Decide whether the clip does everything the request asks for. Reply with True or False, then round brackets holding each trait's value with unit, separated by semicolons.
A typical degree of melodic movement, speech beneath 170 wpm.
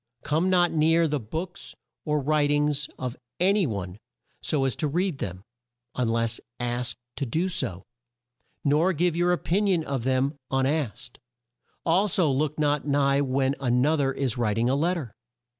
False (4.2 semitones; 185 wpm)